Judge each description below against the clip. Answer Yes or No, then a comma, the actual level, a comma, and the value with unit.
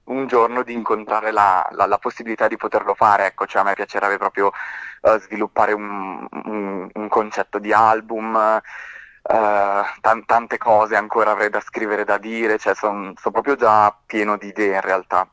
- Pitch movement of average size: No, narrow, 1.5 semitones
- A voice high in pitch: No, low, 105 Hz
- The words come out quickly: Yes, fast, 175 wpm